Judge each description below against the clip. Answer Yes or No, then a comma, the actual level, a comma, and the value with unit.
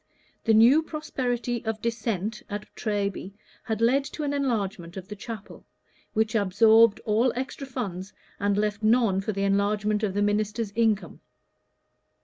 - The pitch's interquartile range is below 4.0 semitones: Yes, narrow, 2.4 semitones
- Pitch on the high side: Yes, high, 215 Hz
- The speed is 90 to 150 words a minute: Yes, average, 145 wpm